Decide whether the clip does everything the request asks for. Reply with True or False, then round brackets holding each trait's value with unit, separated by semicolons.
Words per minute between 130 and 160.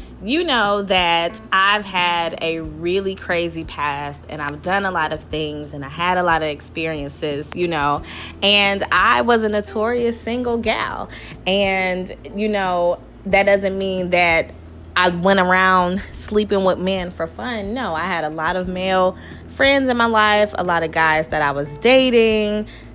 False (175 wpm)